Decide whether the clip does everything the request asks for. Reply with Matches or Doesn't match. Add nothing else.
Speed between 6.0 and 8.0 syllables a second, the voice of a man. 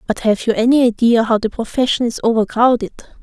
Doesn't match